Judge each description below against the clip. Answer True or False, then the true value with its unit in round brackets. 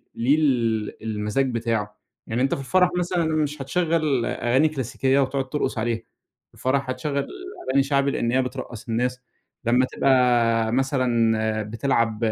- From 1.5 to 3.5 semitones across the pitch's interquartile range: True (3.1 semitones)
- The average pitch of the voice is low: True (130 Hz)